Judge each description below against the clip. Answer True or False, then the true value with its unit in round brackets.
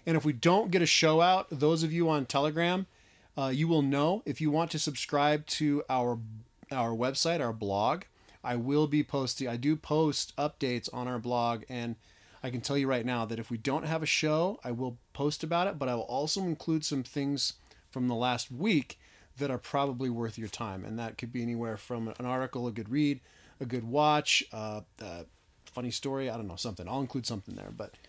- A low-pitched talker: True (130 Hz)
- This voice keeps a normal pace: False (220 wpm)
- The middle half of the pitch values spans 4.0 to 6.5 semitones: True (4.3 semitones)